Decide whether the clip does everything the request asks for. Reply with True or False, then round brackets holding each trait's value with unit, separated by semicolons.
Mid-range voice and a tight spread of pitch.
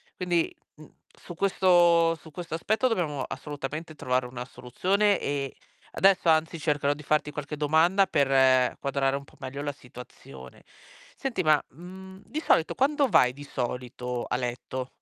False (150 Hz; 4.8 semitones)